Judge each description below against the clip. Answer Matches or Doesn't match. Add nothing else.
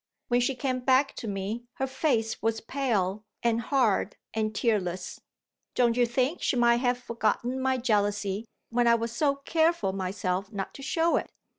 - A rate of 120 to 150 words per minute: Doesn't match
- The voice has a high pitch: Matches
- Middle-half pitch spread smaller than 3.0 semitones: Doesn't match